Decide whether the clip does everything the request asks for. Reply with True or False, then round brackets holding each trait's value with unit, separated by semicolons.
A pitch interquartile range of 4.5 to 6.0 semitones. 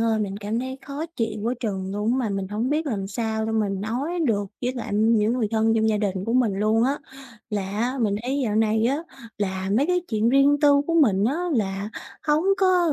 False (4.0 semitones)